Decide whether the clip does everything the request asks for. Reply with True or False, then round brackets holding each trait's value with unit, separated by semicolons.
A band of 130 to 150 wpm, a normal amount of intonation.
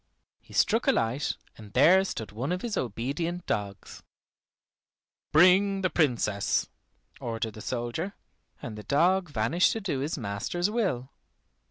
False (140 wpm; 8.3 semitones)